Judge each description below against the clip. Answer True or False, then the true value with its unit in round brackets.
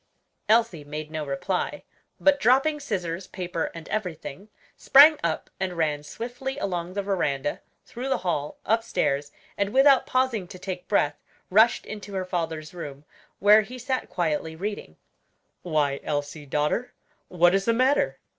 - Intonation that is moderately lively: False (6.7 semitones)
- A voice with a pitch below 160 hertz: False (185 Hz)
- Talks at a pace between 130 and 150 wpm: True (145 wpm)